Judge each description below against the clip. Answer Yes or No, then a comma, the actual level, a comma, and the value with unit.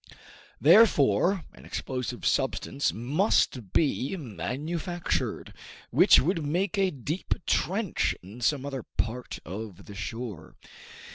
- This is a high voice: No, low, 135 Hz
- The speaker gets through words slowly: Yes, slow, 110 wpm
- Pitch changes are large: Yes, wide, 7.3 semitones